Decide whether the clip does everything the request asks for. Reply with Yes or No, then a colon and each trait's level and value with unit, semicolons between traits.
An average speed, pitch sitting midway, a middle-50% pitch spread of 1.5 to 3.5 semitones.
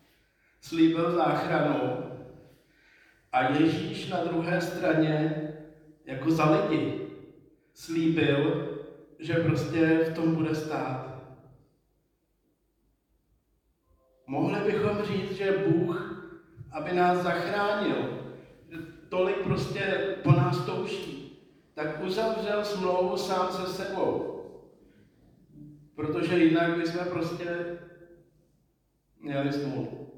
No: slow, 85 wpm; medium, 165 Hz; average, 2.9 semitones